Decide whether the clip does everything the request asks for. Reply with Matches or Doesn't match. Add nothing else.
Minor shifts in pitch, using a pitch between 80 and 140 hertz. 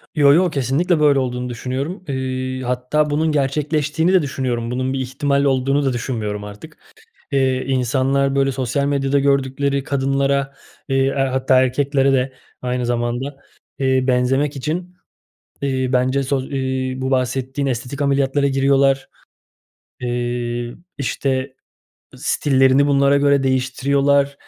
Matches